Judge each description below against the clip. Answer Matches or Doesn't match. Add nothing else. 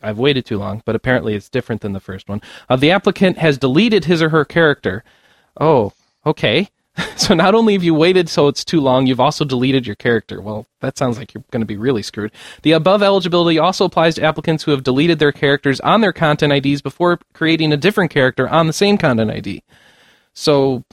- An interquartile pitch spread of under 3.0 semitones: Doesn't match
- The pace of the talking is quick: Matches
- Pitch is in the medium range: Matches